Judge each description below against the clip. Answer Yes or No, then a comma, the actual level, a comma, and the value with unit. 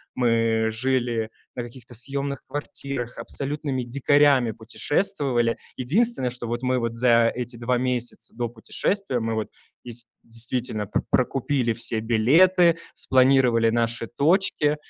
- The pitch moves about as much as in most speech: Yes, average, 3.1 semitones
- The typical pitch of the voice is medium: No, low, 125 Hz